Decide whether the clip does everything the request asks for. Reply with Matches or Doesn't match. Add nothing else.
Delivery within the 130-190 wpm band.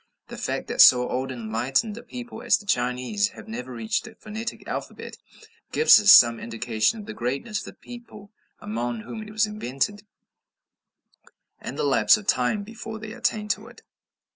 Matches